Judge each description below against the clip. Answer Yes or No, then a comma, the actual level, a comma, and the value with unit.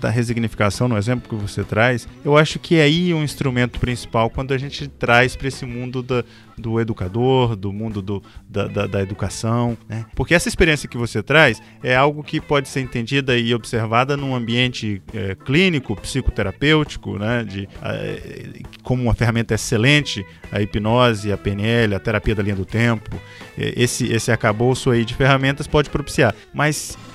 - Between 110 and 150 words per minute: No, average, 170 wpm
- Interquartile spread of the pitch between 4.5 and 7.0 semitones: No, average, 3.9 semitones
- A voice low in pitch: Yes, low, 120 Hz